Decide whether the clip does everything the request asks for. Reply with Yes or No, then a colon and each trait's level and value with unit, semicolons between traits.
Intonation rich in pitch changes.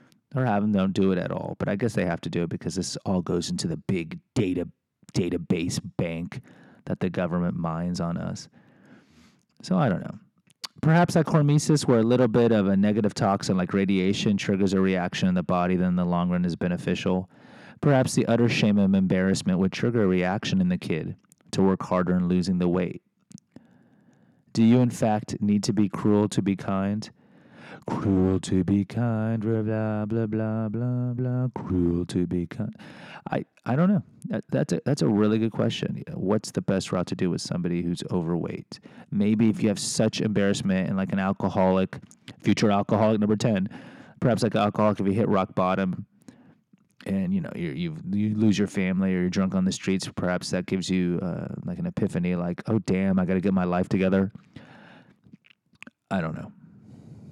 No: average, 4.4 semitones